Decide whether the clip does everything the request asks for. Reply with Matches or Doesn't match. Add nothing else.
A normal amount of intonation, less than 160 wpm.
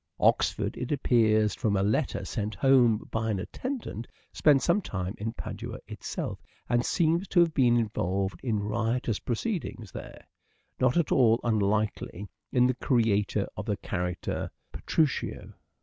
Matches